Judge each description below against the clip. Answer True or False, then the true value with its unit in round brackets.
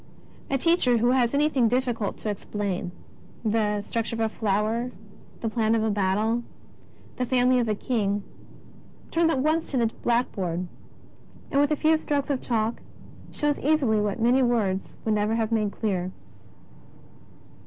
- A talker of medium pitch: False (230 Hz)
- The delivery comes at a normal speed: True (165 wpm)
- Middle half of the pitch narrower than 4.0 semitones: True (3.6 semitones)